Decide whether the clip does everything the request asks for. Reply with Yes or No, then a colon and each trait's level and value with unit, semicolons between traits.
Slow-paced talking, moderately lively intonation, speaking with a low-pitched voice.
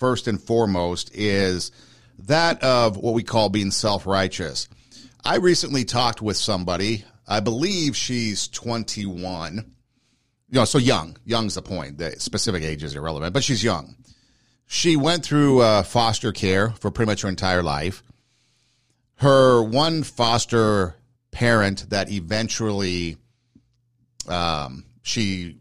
Yes: slow, 130 wpm; average, 4.2 semitones; low, 115 Hz